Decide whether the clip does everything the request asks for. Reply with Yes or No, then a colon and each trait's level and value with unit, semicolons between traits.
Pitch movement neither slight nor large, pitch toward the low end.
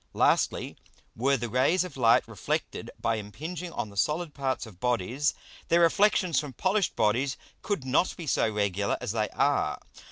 No: wide, 7.2 semitones; low, 130 Hz